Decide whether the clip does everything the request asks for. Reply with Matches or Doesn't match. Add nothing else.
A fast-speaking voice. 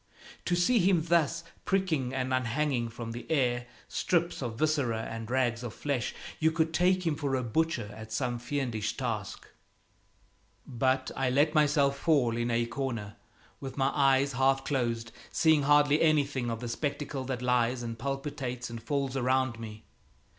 Doesn't match